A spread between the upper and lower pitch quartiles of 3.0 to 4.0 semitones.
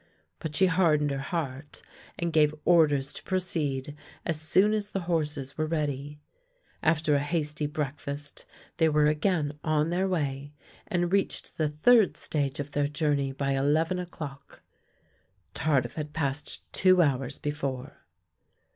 No: narrow, 2.6 semitones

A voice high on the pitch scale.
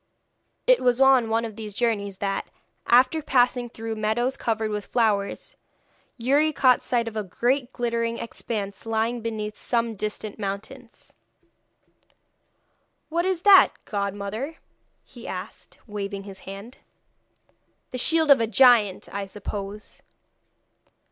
Yes: high, 225 Hz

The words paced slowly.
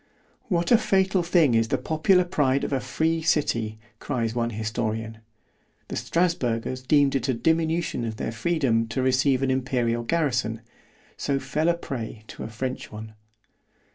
No: average, 150 wpm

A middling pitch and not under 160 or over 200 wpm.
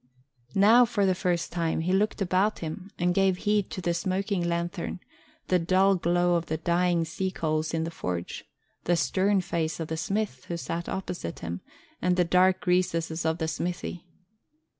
Yes: medium, 175 Hz; average, 180 wpm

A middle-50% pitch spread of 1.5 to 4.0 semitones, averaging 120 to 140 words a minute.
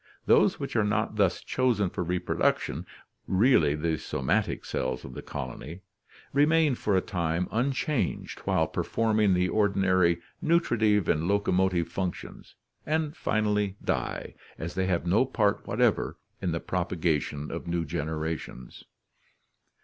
No: average, 4.4 semitones; slow, 135 wpm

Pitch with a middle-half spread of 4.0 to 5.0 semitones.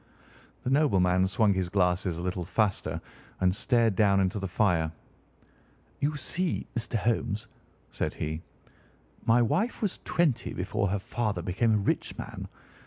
Yes: average, 4.4 semitones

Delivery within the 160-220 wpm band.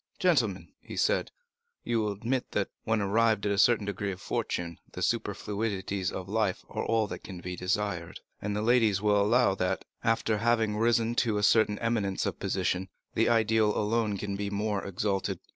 Yes: average, 180 wpm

